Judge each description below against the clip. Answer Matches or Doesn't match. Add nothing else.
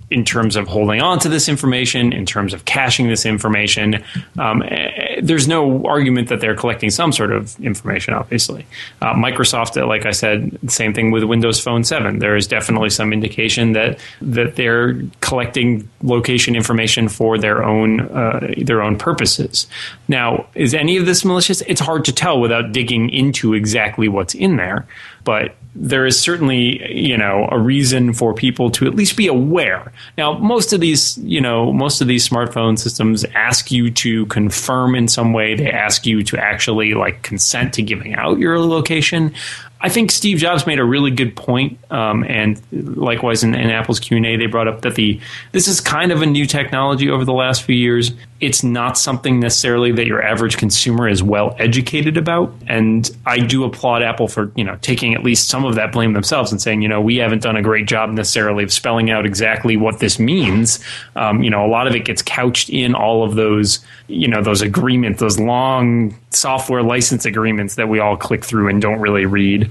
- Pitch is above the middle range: Doesn't match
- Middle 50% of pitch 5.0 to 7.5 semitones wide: Doesn't match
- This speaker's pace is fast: Doesn't match